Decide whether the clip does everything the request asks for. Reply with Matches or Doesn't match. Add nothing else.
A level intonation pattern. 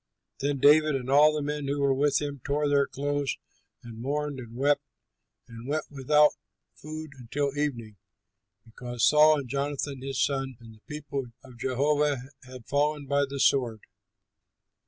Matches